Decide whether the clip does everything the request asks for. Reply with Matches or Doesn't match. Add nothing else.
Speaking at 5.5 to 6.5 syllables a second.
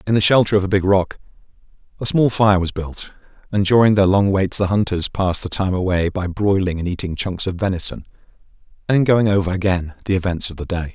Matches